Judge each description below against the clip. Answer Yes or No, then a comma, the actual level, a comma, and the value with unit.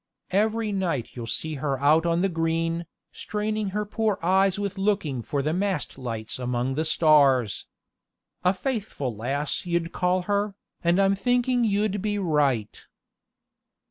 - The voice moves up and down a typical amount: No, wide, 6.1 semitones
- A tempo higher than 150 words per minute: No, average, 145 wpm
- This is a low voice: No, medium, 175 Hz